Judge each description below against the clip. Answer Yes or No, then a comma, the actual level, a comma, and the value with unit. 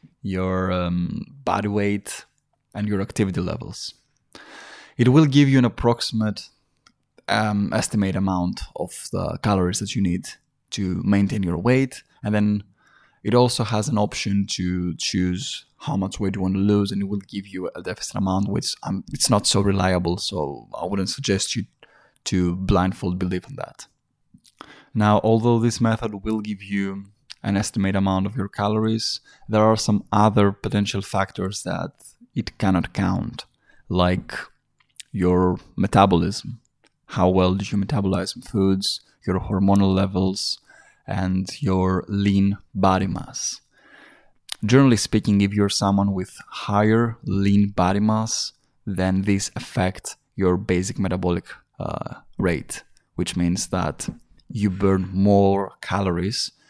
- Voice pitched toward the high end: No, low, 100 Hz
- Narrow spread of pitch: Yes, narrow, 2.2 semitones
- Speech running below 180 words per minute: Yes, average, 140 wpm